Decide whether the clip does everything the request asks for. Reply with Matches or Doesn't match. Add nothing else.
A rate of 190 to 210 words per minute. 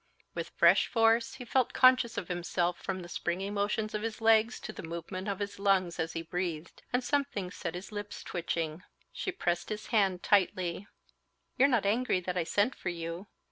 Matches